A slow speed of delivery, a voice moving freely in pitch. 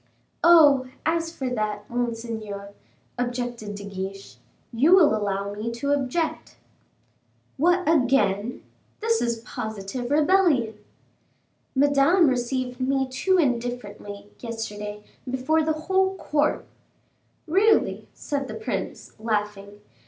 Yes: slow, 105 wpm; wide, 6.4 semitones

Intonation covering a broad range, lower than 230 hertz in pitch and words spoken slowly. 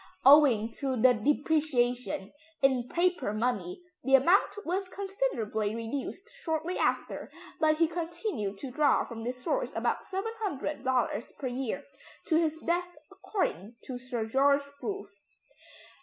No: wide, 6.0 semitones; very high, 275 Hz; slow, 125 wpm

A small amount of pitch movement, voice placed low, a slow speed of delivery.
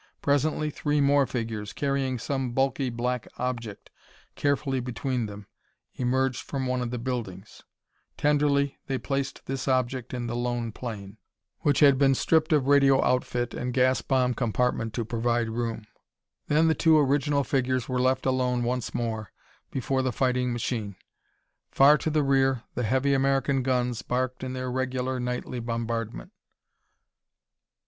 No: narrow, 2.2 semitones; low, 130 Hz; average, 150 wpm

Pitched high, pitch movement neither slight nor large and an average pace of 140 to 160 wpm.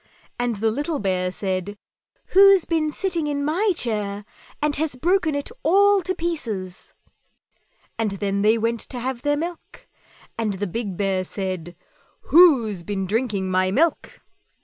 No: high, 230 Hz; wide, 8.2 semitones; average, 150 wpm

